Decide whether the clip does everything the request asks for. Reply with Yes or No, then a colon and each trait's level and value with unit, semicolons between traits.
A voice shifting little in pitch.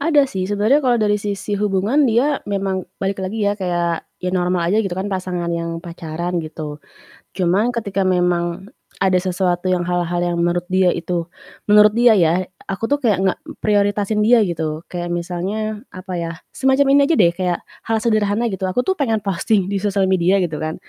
No: average, 3.2 semitones